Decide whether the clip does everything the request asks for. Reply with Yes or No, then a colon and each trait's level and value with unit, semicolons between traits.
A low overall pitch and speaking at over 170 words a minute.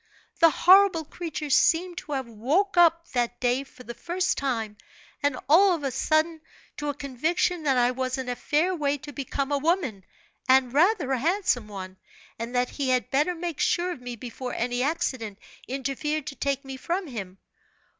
No: very high, 280 Hz; average, 185 wpm